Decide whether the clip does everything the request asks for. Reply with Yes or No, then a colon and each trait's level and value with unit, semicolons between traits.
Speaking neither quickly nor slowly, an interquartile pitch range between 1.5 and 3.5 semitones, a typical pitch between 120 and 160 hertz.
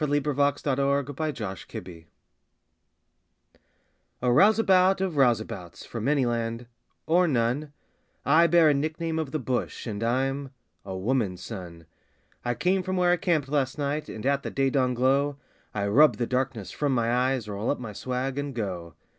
No: average, 170 wpm; average, 4.3 semitones; low, 135 Hz